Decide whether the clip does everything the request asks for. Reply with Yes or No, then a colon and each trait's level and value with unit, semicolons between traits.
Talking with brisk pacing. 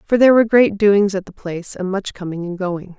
Yes: fast, 260 wpm